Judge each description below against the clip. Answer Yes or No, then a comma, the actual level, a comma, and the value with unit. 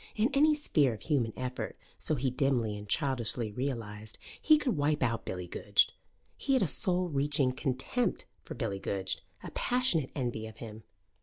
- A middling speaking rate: Yes, average, 170 wpm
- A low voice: Yes, low, 130 Hz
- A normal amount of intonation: No, wide, 6.1 semitones